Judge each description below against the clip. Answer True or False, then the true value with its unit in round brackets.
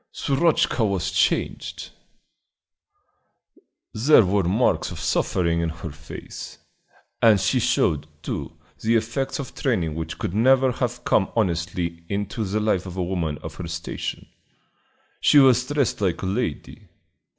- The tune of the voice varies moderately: False (6.3 semitones)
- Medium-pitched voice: False (100 Hz)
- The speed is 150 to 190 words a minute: False (140 wpm)